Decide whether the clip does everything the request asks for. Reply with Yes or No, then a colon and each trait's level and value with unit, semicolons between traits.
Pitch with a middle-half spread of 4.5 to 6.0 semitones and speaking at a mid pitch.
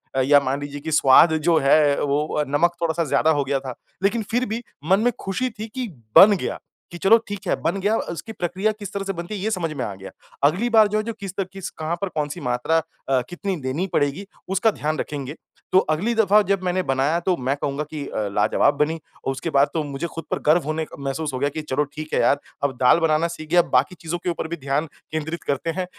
Yes: average, 5.0 semitones; medium, 160 Hz